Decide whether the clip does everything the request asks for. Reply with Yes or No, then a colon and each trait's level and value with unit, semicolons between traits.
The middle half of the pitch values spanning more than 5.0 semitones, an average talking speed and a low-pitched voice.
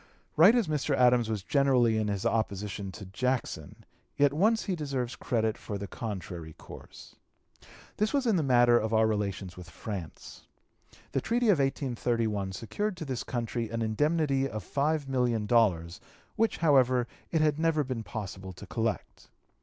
Yes: wide, 5.6 semitones; average, 155 wpm; low, 120 Hz